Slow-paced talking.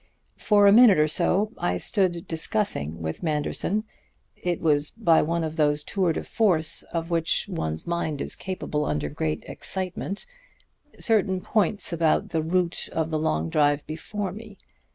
No: average, 155 wpm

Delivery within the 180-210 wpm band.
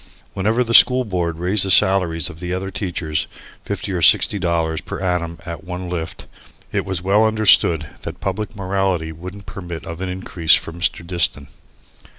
No: average, 170 wpm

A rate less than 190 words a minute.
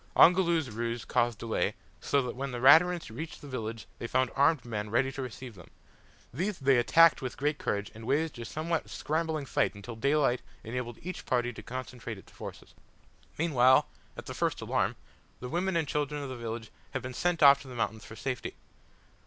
No: average, 195 wpm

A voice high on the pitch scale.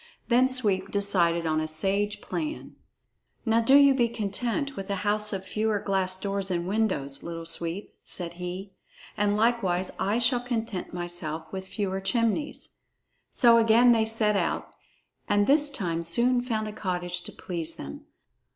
Yes: high, 205 Hz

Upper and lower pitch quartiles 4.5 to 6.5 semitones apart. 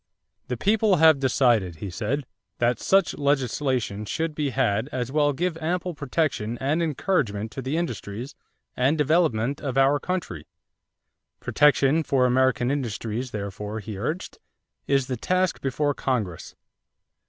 Yes: average, 5.1 semitones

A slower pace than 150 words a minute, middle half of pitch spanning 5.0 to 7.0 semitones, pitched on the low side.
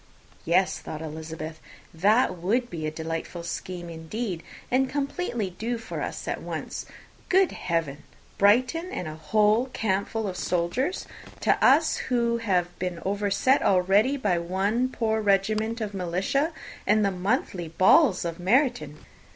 No: average, 140 wpm; average, 5.3 semitones; high, 195 Hz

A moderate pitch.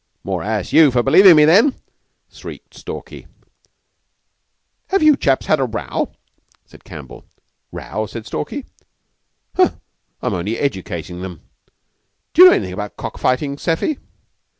No: low, 130 Hz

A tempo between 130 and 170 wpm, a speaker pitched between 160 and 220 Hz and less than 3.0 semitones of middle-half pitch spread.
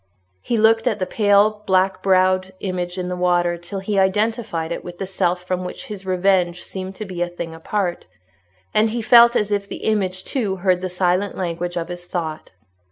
No: average, 200 wpm; medium, 185 Hz; narrow, 2.5 semitones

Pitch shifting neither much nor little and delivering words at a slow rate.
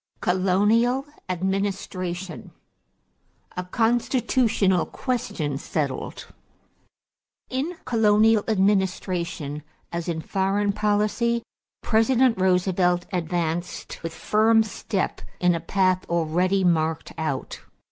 Yes: average, 3.9 semitones; slow, 85 wpm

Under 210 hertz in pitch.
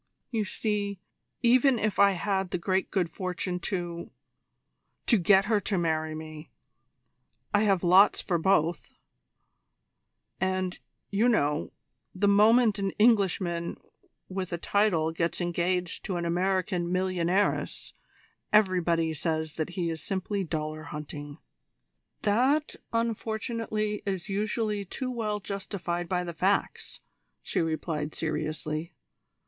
Yes: medium, 185 Hz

